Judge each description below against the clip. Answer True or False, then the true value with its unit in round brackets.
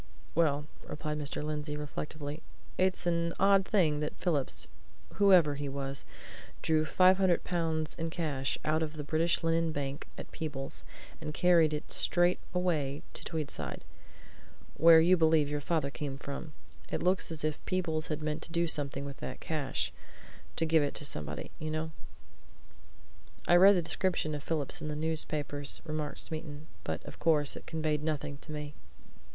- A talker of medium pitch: True (155 Hz)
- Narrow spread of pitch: True (2.2 semitones)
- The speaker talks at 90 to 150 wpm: False (165 wpm)